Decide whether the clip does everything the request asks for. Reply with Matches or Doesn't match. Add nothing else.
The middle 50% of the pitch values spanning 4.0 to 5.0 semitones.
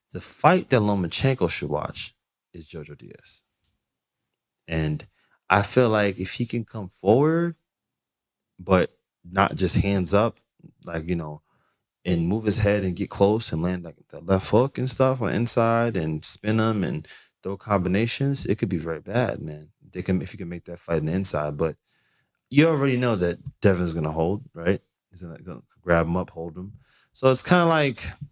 Doesn't match